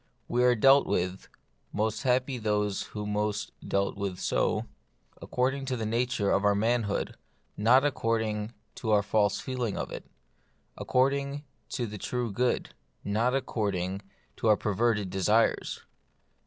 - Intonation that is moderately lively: Yes, average, 3.4 semitones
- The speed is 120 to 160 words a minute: Yes, average, 150 wpm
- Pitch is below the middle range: Yes, low, 110 Hz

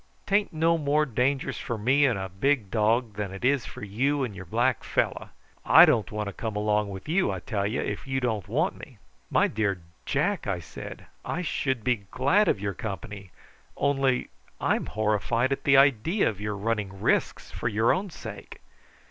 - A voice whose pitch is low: Yes, low, 115 Hz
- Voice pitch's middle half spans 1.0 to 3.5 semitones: No, average, 5.1 semitones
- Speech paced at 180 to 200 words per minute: Yes, average, 190 wpm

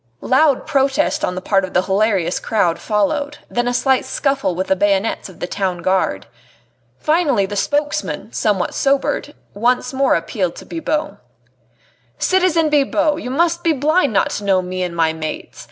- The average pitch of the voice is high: Yes, high, 240 Hz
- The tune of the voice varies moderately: No, wide, 7.6 semitones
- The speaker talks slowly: No, average, 170 wpm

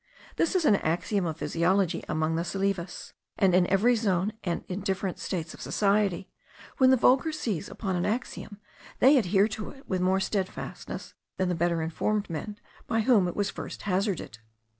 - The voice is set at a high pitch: Yes, high, 195 Hz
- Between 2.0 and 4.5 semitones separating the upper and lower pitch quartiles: Yes, average, 3.2 semitones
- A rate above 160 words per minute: Yes, average, 180 wpm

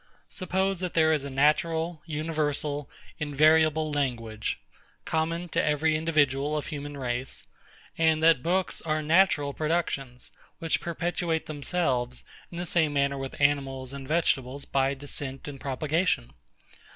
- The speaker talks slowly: Yes, slow, 130 wpm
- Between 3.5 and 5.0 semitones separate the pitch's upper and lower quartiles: No, average, 2.9 semitones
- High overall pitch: No, medium, 150 Hz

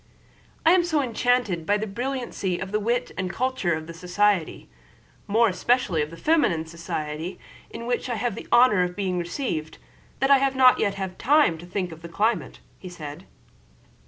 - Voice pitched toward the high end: Yes, high, 200 Hz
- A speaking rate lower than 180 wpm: No, average, 190 wpm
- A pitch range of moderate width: No, wide, 6.3 semitones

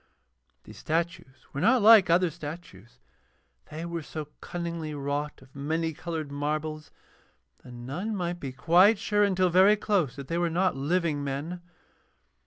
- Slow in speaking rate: No, average, 150 wpm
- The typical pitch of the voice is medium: Yes, medium, 165 Hz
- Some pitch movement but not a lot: Yes, average, 3.8 semitones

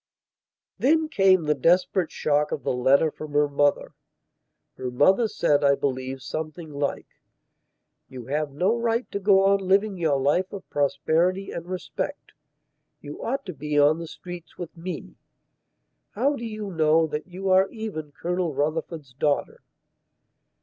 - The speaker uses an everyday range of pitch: Yes, average, 4.8 semitones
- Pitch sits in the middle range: Yes, medium, 165 Hz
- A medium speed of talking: Yes, average, 150 wpm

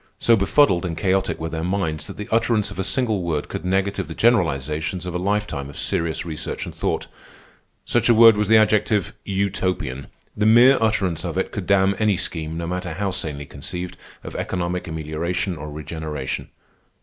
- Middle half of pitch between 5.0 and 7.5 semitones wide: No, average, 4.5 semitones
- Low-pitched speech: Yes, very low, 90 Hz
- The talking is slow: No, average, 185 wpm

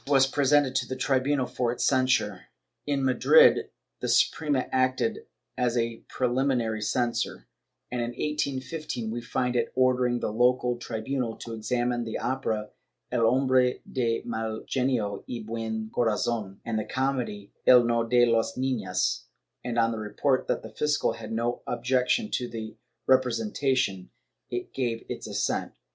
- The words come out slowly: No, average, 150 wpm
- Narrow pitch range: Yes, narrow, 2.3 semitones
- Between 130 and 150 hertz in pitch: No, low, 120 Hz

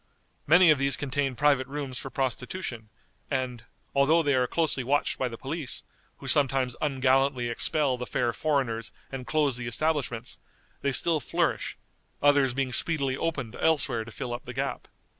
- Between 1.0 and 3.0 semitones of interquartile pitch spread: Yes, narrow, 2.6 semitones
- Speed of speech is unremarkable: Yes, average, 160 wpm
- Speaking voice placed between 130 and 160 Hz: Yes, low, 135 Hz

